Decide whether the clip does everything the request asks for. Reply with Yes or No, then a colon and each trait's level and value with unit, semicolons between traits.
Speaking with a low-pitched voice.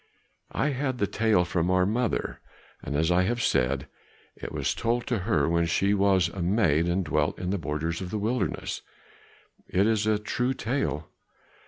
Yes: very low, 95 Hz